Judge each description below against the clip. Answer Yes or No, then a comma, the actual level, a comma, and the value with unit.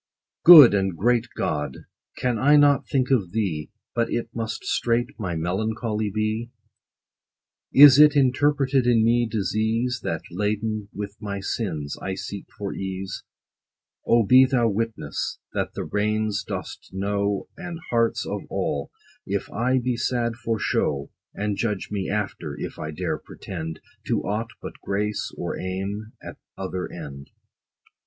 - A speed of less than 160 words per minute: Yes, average, 145 wpm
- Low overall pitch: Yes, low, 110 Hz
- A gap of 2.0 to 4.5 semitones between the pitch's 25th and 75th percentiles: Yes, average, 3.7 semitones